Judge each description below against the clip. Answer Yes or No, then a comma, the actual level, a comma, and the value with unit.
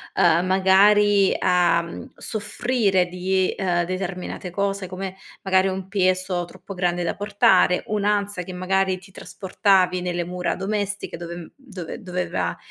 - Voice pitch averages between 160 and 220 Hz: Yes, medium, 185 Hz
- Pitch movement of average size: No, narrow, 1.8 semitones